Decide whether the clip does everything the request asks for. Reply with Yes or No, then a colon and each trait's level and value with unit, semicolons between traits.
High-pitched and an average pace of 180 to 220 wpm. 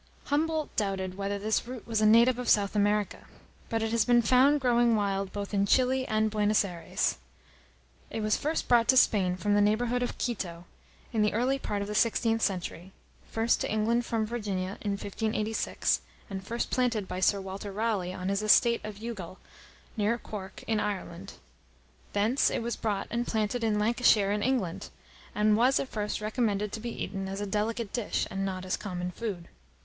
Yes: high, 215 Hz; average, 185 wpm